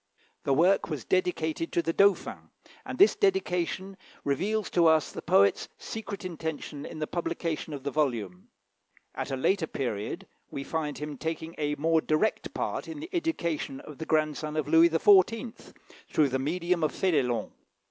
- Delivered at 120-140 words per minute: No, average, 165 wpm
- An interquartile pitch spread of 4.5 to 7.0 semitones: No, average, 3.9 semitones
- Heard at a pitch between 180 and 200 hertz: No, medium, 160 Hz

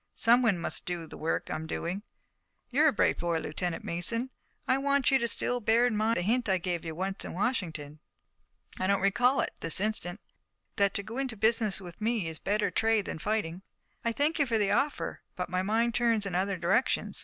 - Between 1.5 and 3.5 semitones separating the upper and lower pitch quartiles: No, average, 4.9 semitones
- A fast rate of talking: Yes, fast, 225 wpm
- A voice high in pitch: Yes, high, 210 Hz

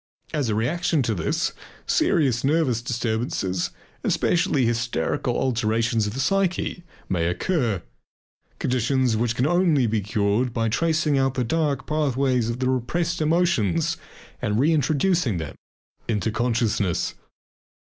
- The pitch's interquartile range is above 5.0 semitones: Yes, wide, 5.4 semitones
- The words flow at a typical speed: No, slow, 125 wpm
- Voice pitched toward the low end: Yes, low, 125 Hz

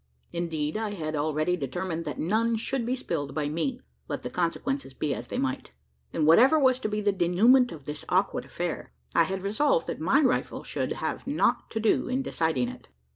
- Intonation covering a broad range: Yes, wide, 8.0 semitones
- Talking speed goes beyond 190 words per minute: Yes, average, 200 wpm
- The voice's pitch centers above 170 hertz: Yes, medium, 185 Hz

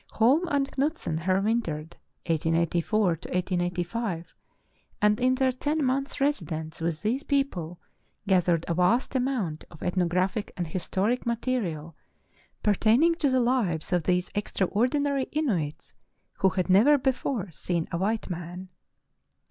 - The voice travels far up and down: Yes, wide, 7.0 semitones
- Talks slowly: Yes, slow, 130 wpm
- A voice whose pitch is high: Yes, high, 200 Hz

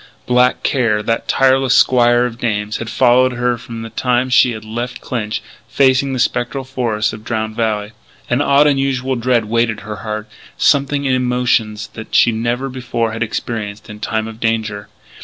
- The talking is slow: No, average, 175 wpm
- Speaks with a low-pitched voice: Yes, low, 120 Hz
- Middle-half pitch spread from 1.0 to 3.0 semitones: Yes, average, 2.7 semitones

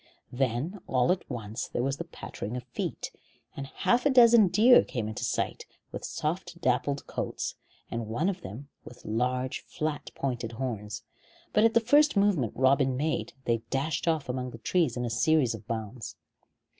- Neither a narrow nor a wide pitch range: No, wide, 6.5 semitones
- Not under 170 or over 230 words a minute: Yes, average, 175 wpm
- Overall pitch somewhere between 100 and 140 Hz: Yes, low, 135 Hz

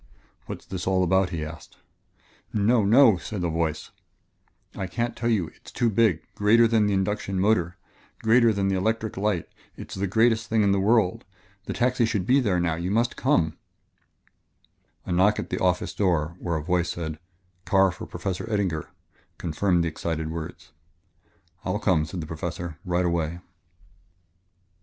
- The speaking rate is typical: Yes, average, 175 wpm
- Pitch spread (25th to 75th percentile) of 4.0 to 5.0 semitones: Yes, average, 4.3 semitones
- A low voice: Yes, very low, 95 Hz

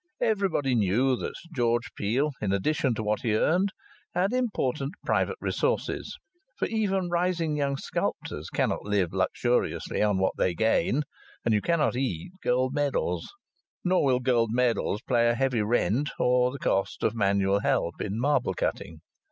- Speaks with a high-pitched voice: No, low, 125 Hz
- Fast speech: No, average, 155 wpm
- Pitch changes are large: Yes, wide, 5.9 semitones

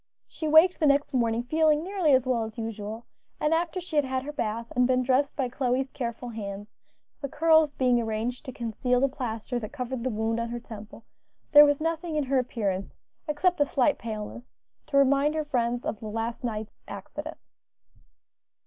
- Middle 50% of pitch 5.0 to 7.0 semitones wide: No, average, 4.3 semitones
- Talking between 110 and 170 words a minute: No, average, 190 wpm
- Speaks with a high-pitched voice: Yes, very high, 255 Hz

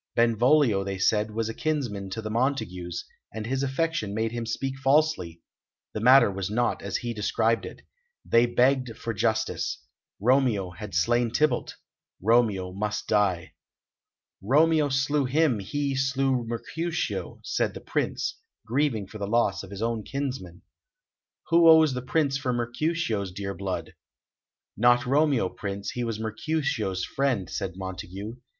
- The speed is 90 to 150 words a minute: Yes, average, 145 wpm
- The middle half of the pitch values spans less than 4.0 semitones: No, average, 5.1 semitones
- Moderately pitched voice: No, low, 115 Hz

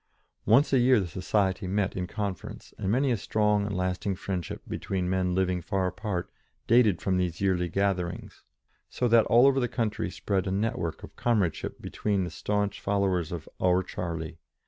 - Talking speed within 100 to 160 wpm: No, average, 180 wpm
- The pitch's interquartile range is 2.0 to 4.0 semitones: Yes, average, 2.7 semitones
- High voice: No, very low, 95 Hz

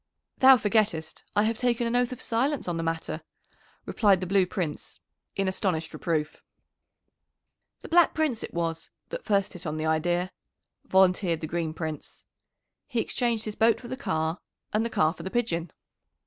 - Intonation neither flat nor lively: No, wide, 5.9 semitones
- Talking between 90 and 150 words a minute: No, average, 175 wpm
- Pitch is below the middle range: No, high, 190 Hz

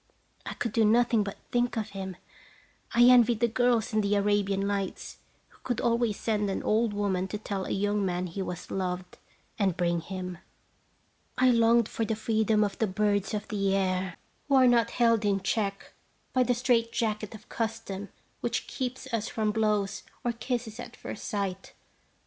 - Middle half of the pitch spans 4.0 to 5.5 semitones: No, average, 2.9 semitones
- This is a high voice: Yes, high, 210 Hz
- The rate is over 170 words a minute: Yes, average, 180 wpm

